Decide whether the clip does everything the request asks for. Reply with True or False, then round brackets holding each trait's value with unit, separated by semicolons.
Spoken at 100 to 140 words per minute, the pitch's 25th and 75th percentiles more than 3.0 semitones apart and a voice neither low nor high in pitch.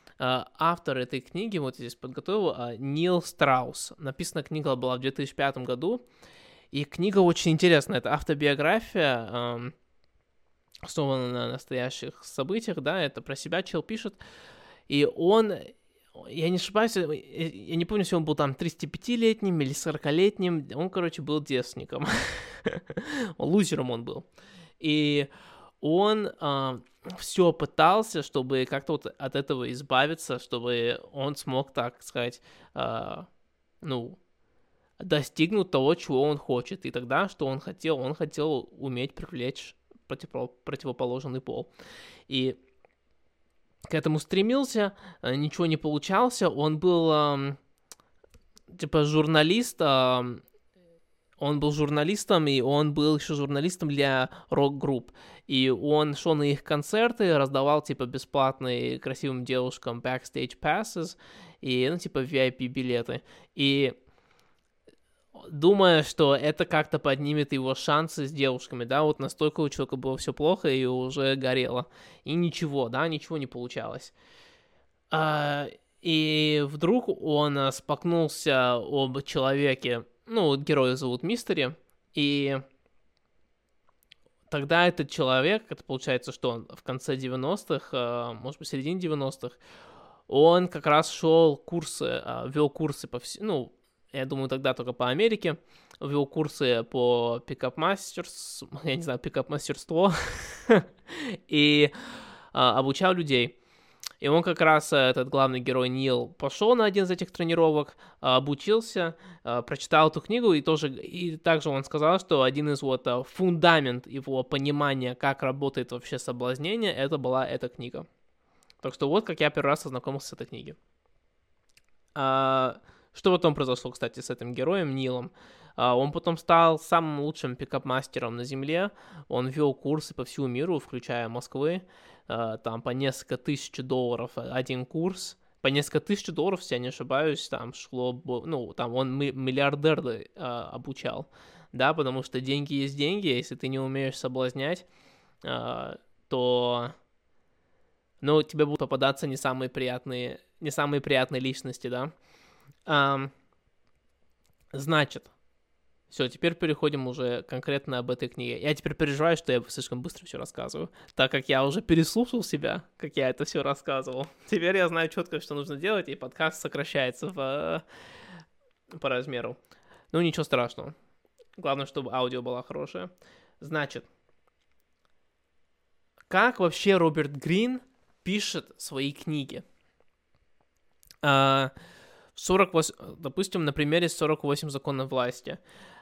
True (125 wpm; 4.2 semitones; 145 Hz)